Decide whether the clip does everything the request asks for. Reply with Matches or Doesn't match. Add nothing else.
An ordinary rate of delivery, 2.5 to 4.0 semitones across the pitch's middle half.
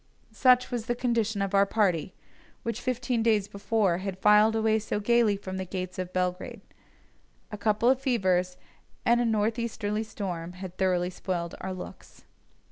Matches